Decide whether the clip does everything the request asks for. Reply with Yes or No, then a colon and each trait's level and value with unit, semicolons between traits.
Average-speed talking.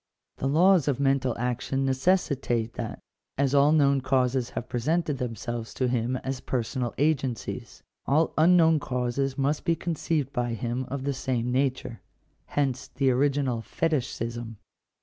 Yes: average, 145 wpm